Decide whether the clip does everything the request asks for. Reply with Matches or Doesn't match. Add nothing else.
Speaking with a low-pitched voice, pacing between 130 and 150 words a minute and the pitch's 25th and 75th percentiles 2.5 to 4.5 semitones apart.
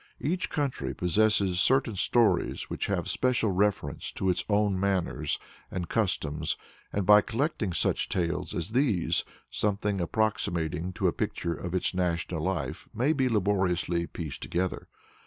Matches